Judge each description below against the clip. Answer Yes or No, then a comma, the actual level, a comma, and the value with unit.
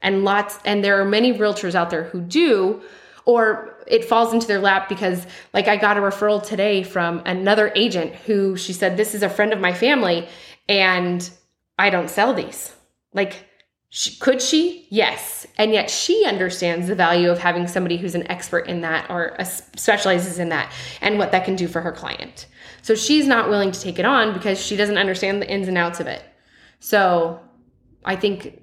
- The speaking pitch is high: Yes, high, 195 Hz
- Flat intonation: No, average, 3.0 semitones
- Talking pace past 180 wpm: Yes, average, 200 wpm